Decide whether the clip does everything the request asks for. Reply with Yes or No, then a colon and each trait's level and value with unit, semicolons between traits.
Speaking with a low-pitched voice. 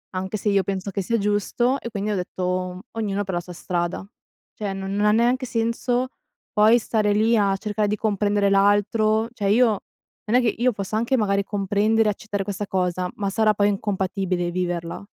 No: high, 205 Hz